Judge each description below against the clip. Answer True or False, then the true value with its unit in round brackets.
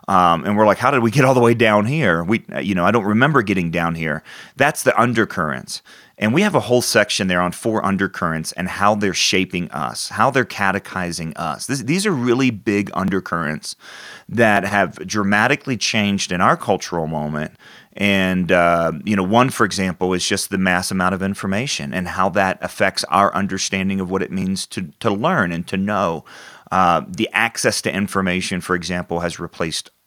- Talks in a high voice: False (95 Hz)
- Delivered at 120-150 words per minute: False (195 wpm)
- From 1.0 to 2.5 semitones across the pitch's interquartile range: False (2.9 semitones)